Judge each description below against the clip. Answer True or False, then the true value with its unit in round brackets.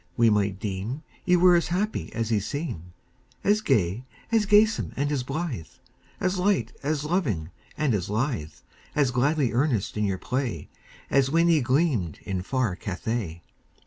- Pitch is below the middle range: True (130 Hz)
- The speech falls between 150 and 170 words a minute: True (155 wpm)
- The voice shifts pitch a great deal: True (8.0 semitones)